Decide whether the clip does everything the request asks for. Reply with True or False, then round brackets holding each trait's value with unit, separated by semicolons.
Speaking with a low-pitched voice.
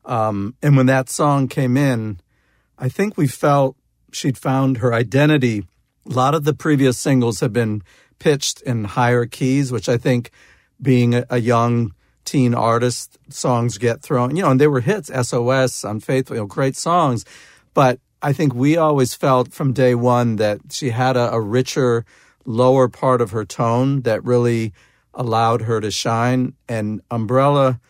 True (125 Hz)